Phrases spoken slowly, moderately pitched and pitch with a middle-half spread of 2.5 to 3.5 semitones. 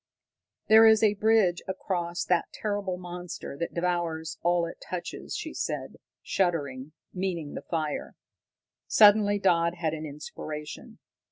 Yes: slow, 125 wpm; medium, 175 Hz; average, 3.1 semitones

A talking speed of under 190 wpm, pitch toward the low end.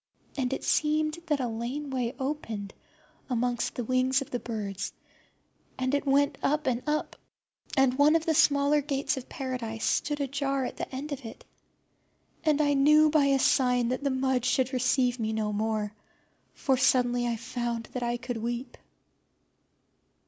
No: average, 170 wpm; very high, 260 Hz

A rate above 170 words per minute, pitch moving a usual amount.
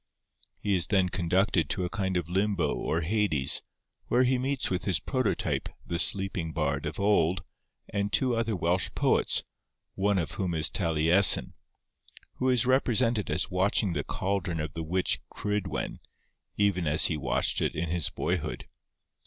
No: average, 160 wpm; average, 3.6 semitones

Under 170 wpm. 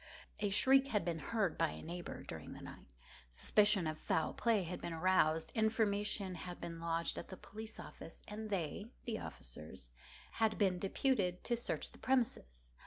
No: average, 175 wpm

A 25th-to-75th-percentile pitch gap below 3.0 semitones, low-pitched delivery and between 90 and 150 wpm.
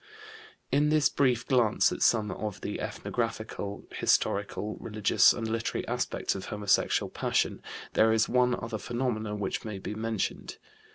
Yes: narrow, 2.4 semitones; low, 110 Hz; average, 145 wpm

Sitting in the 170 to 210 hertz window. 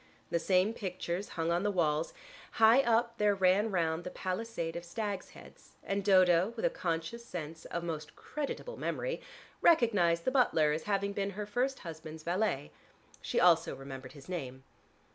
Yes: medium, 185 Hz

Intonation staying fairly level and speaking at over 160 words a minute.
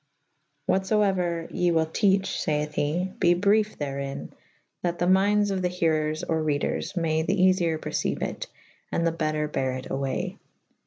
No: average, 3.5 semitones; average, 175 wpm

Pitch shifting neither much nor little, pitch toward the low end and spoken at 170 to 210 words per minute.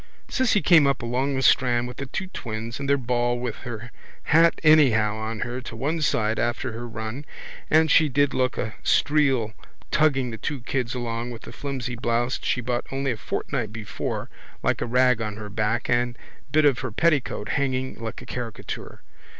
Yes: average, 3.3 semitones; low, 125 Hz; average, 190 wpm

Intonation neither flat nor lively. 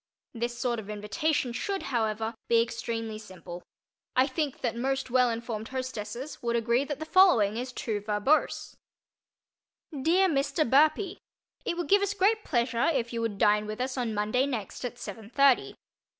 Yes: average, 4.0 semitones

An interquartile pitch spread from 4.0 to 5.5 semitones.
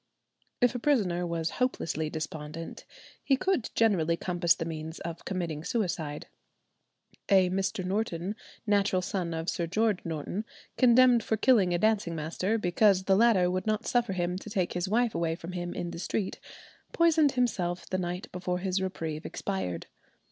Yes: average, 4.3 semitones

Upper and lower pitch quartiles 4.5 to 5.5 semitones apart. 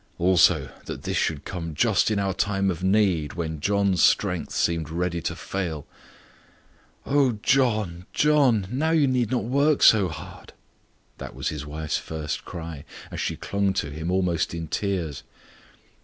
Yes: average, 4.9 semitones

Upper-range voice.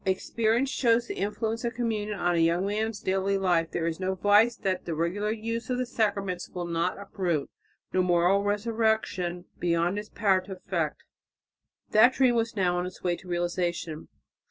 Yes: high, 195 Hz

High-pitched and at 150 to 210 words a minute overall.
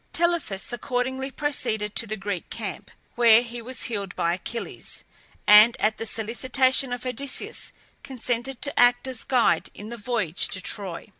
Yes: high, 235 Hz; average, 155 wpm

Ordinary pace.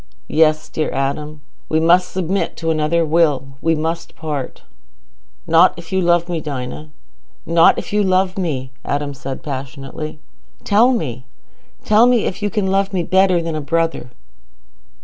Yes: average, 150 wpm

